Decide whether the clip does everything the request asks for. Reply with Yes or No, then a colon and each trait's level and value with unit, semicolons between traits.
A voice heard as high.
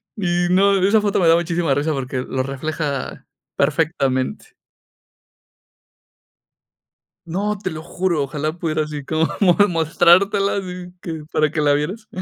No: medium, 165 Hz